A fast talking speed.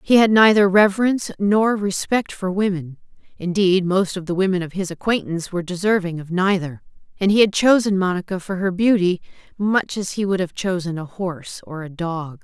No: average, 180 wpm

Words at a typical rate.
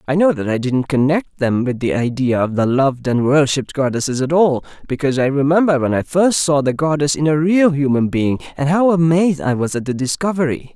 No: fast, 225 wpm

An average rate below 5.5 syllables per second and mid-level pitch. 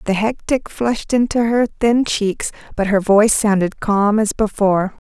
No: 4.7 syllables/s; high, 215 Hz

